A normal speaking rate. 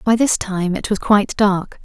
No: fast, 230 wpm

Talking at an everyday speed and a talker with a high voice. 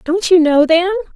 No: fast, 210 wpm; very high, 340 Hz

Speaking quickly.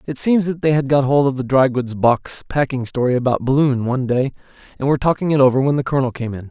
Yes: fast, 260 wpm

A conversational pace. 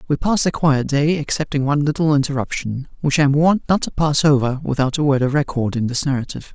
No: fast, 230 wpm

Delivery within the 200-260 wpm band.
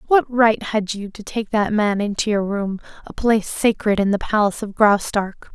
Yes: fast, 205 wpm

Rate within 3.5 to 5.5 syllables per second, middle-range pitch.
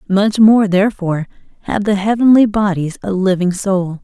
No: 5.0 syllables/s; high, 195 Hz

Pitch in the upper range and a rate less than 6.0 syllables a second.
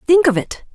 Yes: very high, 295 Hz; 5.4 syllables/s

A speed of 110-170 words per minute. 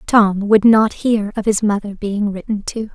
No: fast, 205 wpm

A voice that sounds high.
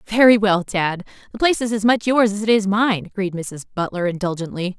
Yes: high, 200 Hz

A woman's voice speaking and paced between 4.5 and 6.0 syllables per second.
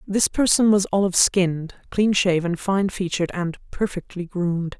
Yes: female; 5.0 syllables/s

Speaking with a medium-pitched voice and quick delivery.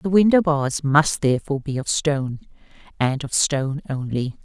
No: medium, 145 Hz; average, 160 wpm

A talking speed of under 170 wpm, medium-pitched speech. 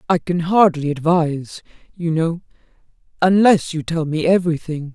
Yes: slow, 135 wpm; medium, 165 Hz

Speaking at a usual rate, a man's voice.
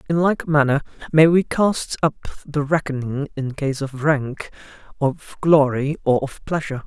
Yes: average, 155 wpm; male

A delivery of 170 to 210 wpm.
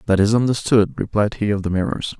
No: fast, 220 wpm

